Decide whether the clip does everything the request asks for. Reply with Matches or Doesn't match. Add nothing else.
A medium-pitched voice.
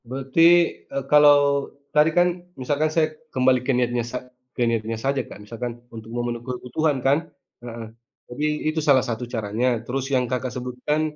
Doesn't match